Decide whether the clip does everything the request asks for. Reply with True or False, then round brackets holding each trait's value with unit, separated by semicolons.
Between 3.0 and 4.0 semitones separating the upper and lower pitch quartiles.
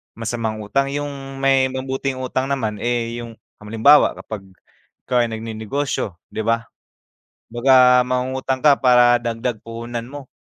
False (2.6 semitones)